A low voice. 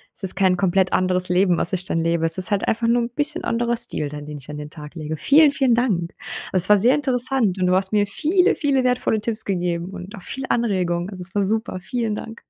No: high, 195 Hz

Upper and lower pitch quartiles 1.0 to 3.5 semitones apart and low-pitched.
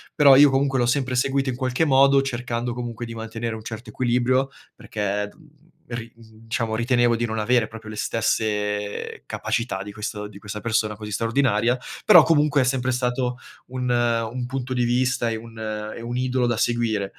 Yes: narrow, 2.5 semitones; low, 120 Hz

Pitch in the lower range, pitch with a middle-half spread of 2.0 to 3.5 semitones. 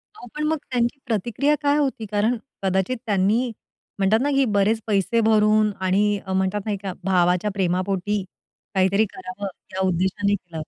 No: high, 205 Hz; average, 3.2 semitones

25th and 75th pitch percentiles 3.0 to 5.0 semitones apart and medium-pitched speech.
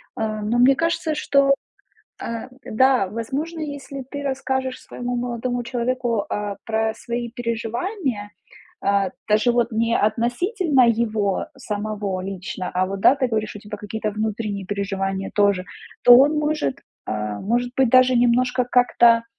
No: average, 3.6 semitones; high, 235 Hz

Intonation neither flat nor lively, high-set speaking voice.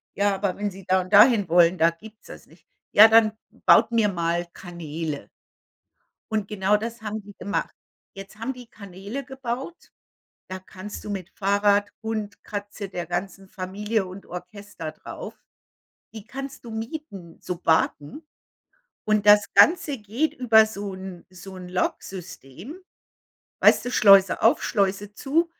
Yes: average, 3.0 semitones; high, 205 Hz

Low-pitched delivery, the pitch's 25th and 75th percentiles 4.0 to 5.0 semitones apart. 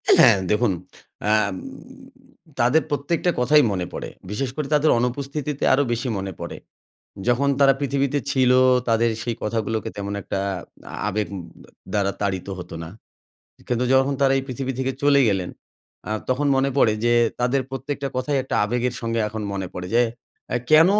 Yes: low, 125 Hz; average, 4.4 semitones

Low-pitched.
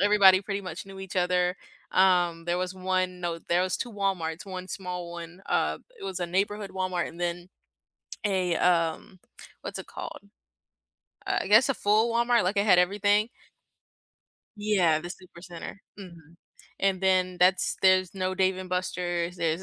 No: medium, 185 Hz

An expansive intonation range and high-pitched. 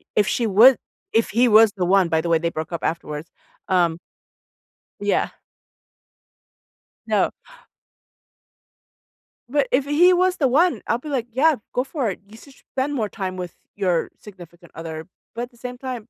Yes: wide, 6.9 semitones; high, 220 Hz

